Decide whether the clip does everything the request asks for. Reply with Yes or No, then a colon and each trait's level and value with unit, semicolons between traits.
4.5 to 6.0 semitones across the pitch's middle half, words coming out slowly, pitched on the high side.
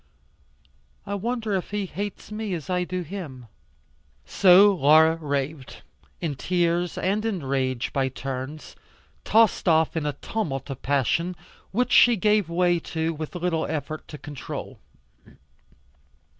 No: average, 5.3 semitones; slow, 130 wpm; medium, 170 Hz